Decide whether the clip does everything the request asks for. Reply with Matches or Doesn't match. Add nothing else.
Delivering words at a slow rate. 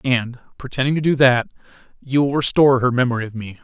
Doesn't match